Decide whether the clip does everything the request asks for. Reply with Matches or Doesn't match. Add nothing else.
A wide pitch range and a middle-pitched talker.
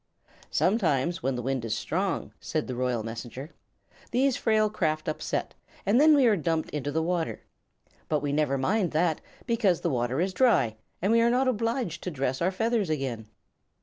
Matches